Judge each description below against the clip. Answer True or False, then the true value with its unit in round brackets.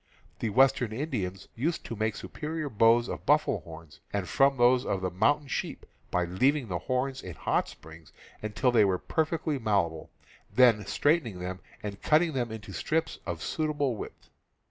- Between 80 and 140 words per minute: False (175 wpm)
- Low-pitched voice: True (115 Hz)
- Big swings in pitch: True (6.7 semitones)